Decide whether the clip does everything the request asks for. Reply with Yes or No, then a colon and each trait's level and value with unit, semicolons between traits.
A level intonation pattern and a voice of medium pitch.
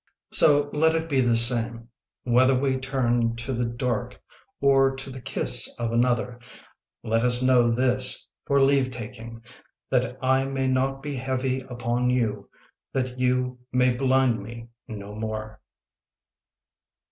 No: narrow, 2.1 semitones; low, 125 Hz